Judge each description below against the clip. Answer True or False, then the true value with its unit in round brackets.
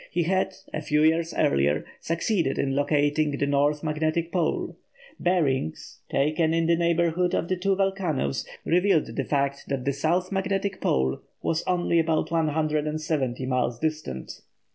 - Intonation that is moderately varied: True (3.4 semitones)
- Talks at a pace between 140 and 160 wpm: True (145 wpm)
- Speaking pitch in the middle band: True (155 Hz)